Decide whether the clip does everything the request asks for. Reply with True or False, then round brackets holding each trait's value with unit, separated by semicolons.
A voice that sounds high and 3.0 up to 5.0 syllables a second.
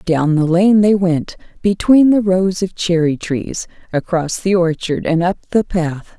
False (180 Hz; 4.1 syllables/s)